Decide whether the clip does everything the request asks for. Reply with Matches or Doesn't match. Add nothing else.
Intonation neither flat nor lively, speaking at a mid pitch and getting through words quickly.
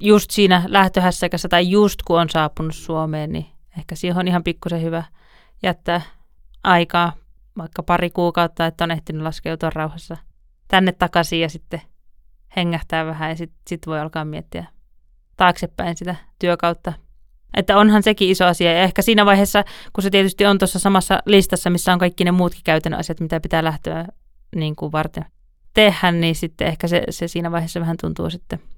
Doesn't match